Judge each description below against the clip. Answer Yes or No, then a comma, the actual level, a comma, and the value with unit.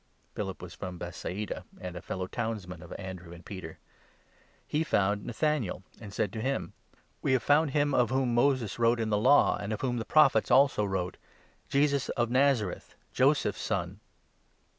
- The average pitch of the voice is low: Yes, low, 110 Hz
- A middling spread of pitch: No, wide, 6.0 semitones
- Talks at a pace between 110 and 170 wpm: No, average, 185 wpm